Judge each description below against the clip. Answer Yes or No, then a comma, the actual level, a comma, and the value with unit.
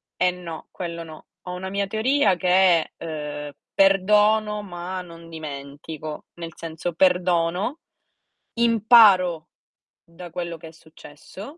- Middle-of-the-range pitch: Yes, medium, 175 Hz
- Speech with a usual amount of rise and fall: Yes, average, 3.0 semitones